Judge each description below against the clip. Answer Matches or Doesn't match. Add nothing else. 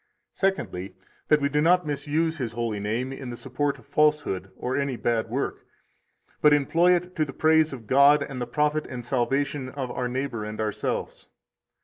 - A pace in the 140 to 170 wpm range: Doesn't match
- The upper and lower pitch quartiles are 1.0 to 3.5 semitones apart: Doesn't match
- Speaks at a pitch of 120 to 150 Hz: Matches